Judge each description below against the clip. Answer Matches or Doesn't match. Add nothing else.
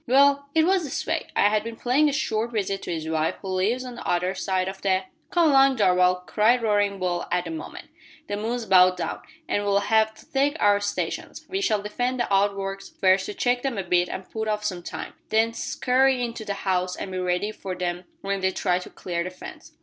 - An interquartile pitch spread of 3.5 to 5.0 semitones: Matches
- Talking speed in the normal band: Doesn't match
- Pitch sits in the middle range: Doesn't match